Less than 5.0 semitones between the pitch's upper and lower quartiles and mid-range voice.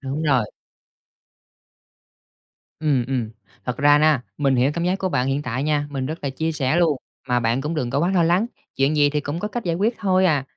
Yes: average, 3.9 semitones; medium, 145 Hz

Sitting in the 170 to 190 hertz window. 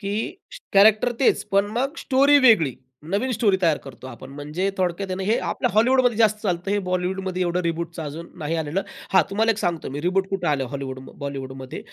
Yes: medium, 185 Hz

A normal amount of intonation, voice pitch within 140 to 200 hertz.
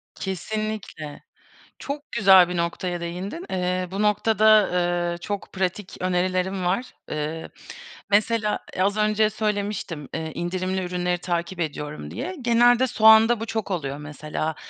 Yes: average, 3.6 semitones; medium, 185 Hz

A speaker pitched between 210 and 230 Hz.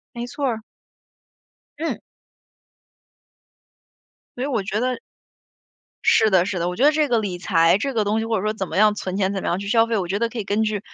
Yes: high, 215 Hz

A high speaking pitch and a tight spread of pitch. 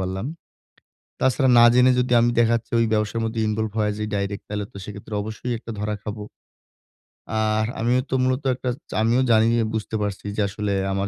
No: low, 110 Hz; narrow, 2.1 semitones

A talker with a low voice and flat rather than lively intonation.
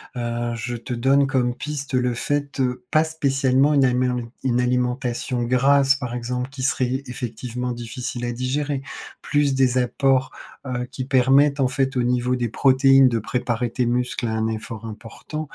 Yes: low, 125 Hz; narrow, 1.8 semitones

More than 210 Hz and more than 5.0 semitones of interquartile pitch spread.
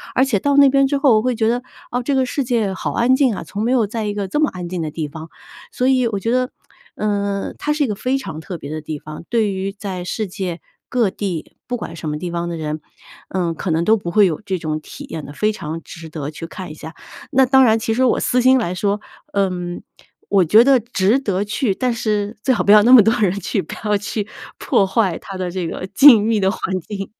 No: high, 205 Hz; wide, 5.4 semitones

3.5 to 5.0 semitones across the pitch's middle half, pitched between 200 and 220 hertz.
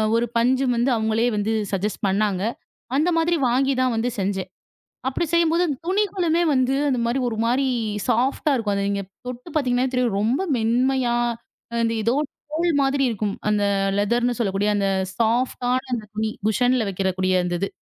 No: average, 4.0 semitones; high, 240 Hz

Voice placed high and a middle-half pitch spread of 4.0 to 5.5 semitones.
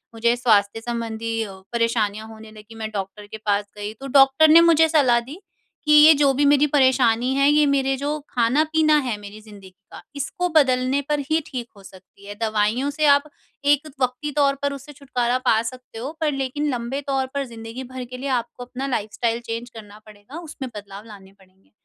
Yes: very high, 250 Hz; average, 4.3 semitones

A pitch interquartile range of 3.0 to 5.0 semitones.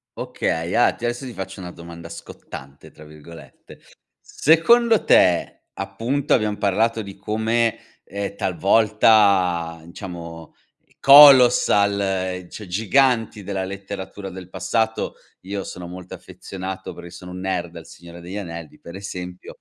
Yes: average, 4.0 semitones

